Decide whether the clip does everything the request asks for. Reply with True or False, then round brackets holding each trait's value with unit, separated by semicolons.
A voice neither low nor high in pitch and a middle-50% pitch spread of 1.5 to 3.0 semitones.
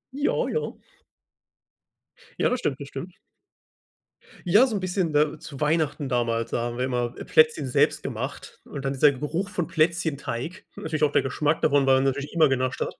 False (150 Hz; 4.2 semitones)